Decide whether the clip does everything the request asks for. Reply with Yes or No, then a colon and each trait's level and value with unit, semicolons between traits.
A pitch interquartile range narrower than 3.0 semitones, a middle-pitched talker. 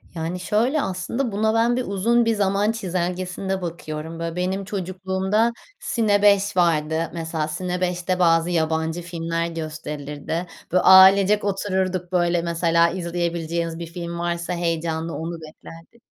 Yes: narrow, 2.6 semitones; medium, 175 Hz